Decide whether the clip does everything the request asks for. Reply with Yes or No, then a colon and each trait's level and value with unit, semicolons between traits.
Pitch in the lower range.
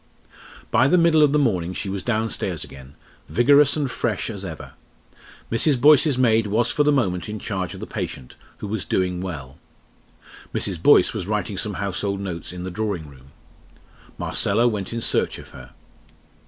Yes: low, 105 Hz